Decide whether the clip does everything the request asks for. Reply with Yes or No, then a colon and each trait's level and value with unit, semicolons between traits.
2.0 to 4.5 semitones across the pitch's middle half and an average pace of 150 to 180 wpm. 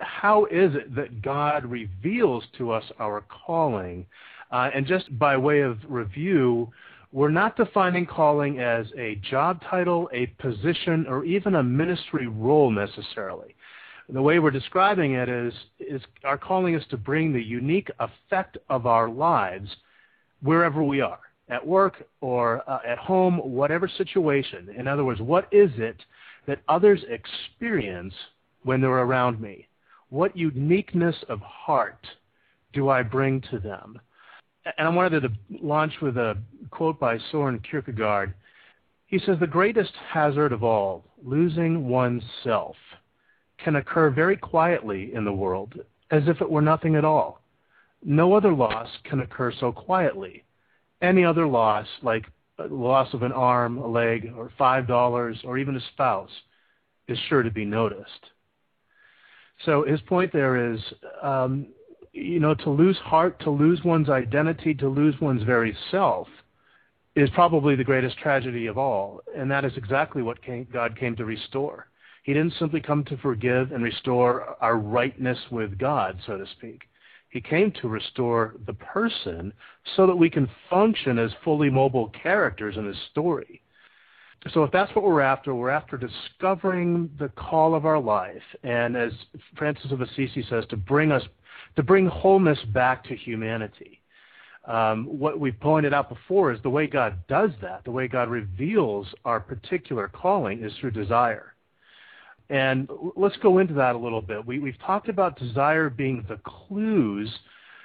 No: average, 5.3 semitones; average, 160 wpm